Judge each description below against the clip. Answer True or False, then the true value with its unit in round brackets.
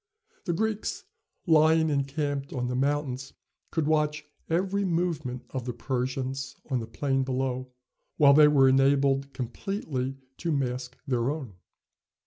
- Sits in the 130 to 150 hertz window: True (140 Hz)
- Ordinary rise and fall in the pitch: True (3.1 semitones)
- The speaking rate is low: True (130 wpm)